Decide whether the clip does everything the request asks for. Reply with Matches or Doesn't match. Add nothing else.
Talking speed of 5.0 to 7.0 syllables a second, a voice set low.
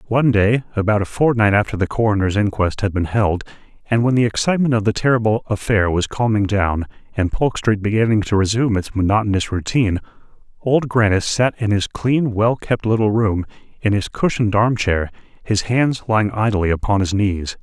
Matches